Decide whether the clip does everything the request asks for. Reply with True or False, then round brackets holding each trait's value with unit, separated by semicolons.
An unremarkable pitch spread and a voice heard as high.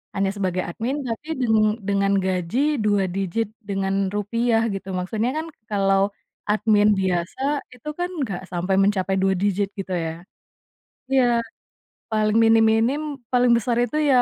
True (3.1 semitones; 205 Hz)